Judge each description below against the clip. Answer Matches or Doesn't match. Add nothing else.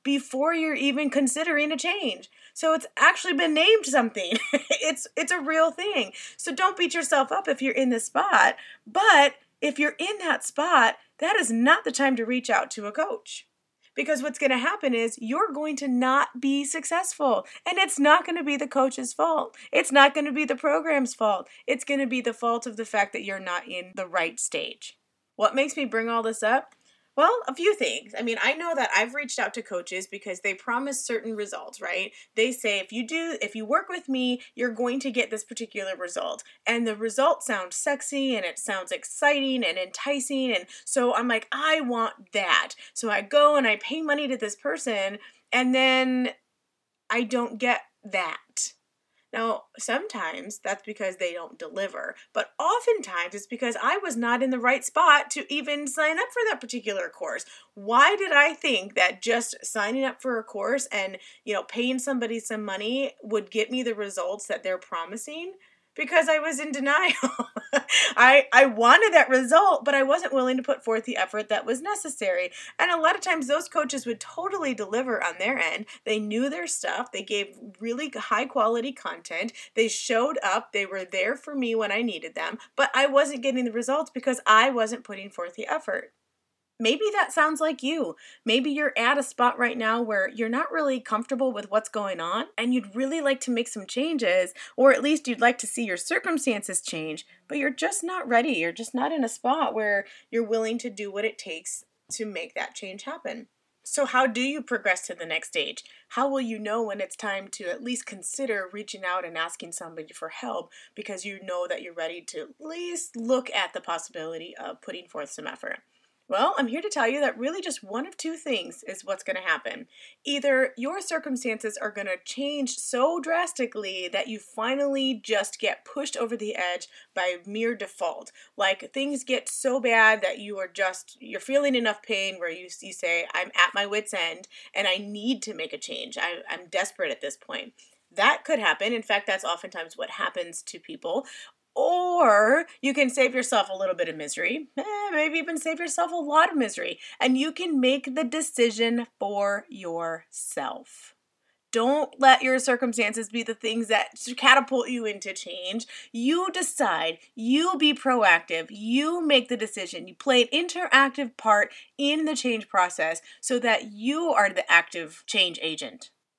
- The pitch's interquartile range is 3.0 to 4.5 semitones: Doesn't match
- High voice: Matches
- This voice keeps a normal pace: Matches